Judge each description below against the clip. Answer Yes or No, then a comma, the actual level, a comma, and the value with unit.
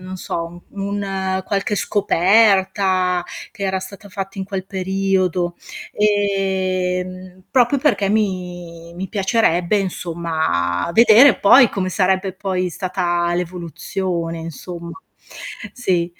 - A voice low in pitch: No, medium, 185 Hz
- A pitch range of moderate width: No, narrow, 2.0 semitones